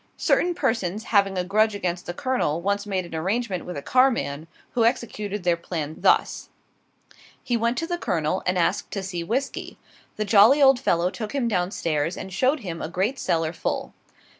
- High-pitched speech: Yes, high, 195 Hz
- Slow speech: No, average, 190 wpm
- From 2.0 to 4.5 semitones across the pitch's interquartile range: No, average, 5.2 semitones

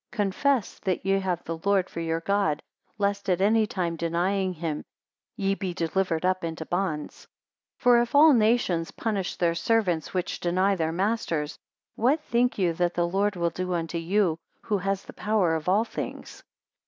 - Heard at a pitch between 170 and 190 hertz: Yes, medium, 185 Hz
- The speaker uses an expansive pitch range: No, average, 3.3 semitones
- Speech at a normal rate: Yes, average, 180 wpm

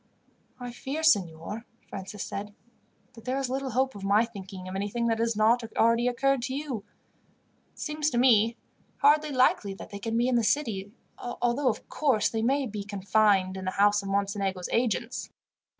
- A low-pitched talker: No, high, 225 Hz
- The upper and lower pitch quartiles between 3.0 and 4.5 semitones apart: Yes, average, 4.1 semitones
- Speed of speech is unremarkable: Yes, average, 180 wpm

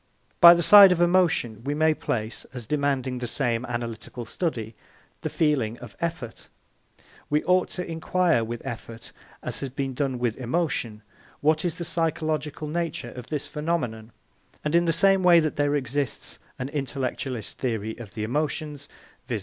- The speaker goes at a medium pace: Yes, average, 165 wpm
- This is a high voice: No, medium, 145 Hz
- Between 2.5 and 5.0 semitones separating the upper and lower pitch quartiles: No, wide, 5.4 semitones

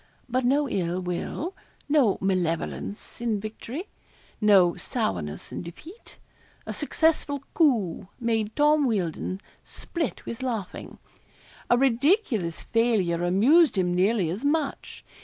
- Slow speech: Yes, slow, 115 wpm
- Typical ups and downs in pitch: No, wide, 7.4 semitones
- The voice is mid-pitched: No, high, 225 Hz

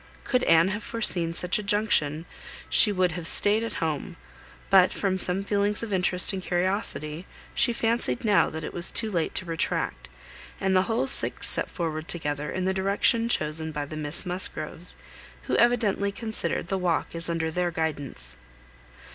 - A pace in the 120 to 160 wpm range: No, average, 170 wpm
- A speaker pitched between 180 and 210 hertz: Yes, medium, 185 Hz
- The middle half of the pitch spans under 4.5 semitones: Yes, average, 4.1 semitones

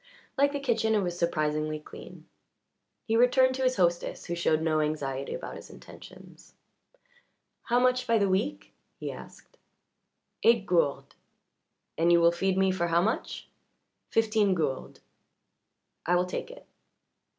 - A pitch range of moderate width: No, wide, 5.9 semitones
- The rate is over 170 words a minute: No, average, 145 wpm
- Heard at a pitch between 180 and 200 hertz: Yes, medium, 185 Hz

